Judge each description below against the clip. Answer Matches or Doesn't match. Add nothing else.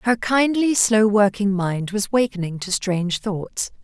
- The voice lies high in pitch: Matches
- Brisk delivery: Doesn't match